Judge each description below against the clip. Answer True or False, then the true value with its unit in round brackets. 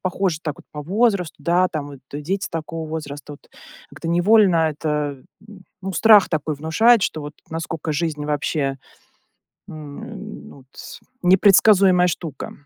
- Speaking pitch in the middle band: True (165 Hz)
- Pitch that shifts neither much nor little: True (4.1 semitones)